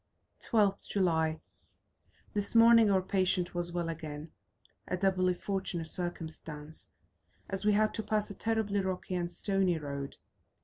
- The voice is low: No, medium, 185 Hz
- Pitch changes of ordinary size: Yes, average, 3.4 semitones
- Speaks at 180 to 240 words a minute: No, slow, 135 wpm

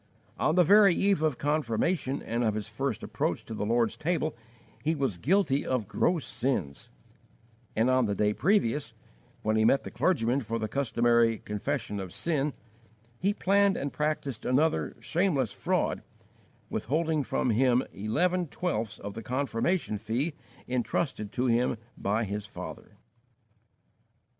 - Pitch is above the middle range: No, low, 130 Hz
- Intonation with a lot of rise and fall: Yes, wide, 5.9 semitones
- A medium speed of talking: Yes, average, 145 wpm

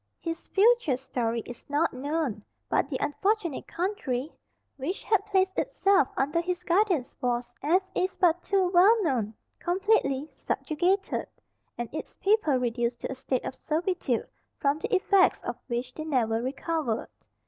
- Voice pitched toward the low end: No, very high, 315 Hz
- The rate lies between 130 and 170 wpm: Yes, average, 150 wpm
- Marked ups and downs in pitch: Yes, wide, 6.8 semitones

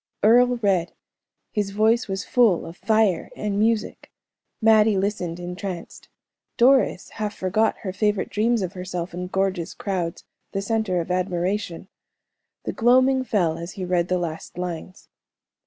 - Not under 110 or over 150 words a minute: Yes, average, 140 wpm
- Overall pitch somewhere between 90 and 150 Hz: No, high, 195 Hz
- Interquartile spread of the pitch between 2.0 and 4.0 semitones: Yes, average, 3.4 semitones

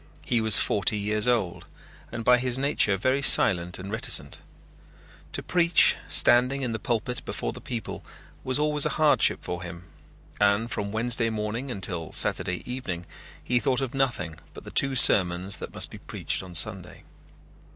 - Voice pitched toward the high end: No, low, 115 Hz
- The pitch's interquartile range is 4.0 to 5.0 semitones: Yes, average, 4.7 semitones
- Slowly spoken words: No, average, 165 wpm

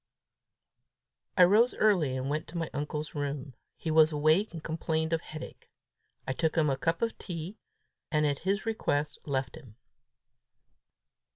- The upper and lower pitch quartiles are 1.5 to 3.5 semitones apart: Yes, average, 2.9 semitones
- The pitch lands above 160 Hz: No, medium, 155 Hz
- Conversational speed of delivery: Yes, average, 155 wpm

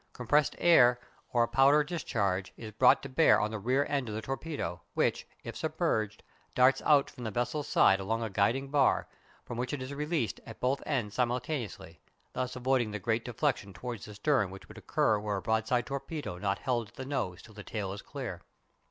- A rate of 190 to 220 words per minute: Yes, fast, 205 wpm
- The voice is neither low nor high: No, low, 120 Hz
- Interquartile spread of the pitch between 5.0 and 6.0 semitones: No, average, 4.3 semitones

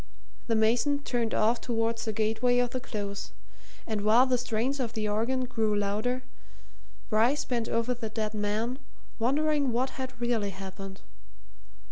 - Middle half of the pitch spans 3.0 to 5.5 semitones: No, narrow, 2.6 semitones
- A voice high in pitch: Yes, high, 230 Hz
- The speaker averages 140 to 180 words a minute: Yes, average, 150 wpm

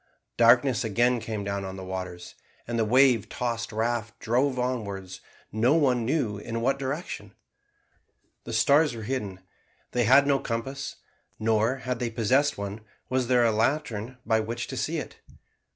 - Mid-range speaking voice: No, low, 120 Hz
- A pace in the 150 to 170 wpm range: Yes, average, 160 wpm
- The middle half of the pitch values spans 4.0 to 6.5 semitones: No, average, 3.1 semitones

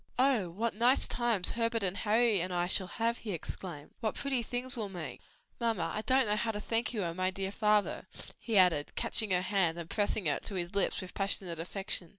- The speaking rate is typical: No, fast, 215 wpm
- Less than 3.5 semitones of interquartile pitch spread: No, average, 4.1 semitones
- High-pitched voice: Yes, high, 205 Hz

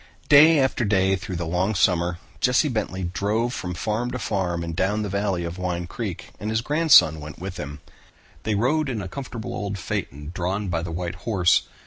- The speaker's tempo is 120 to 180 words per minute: No, average, 200 wpm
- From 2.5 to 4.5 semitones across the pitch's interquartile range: Yes, average, 4.2 semitones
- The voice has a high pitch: No, very low, 95 Hz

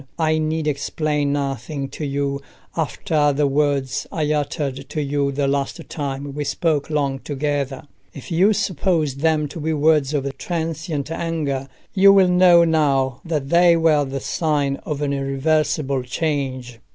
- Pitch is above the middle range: No, medium, 145 Hz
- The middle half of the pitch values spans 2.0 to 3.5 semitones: Yes, narrow, 2.5 semitones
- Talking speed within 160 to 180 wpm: No, average, 150 wpm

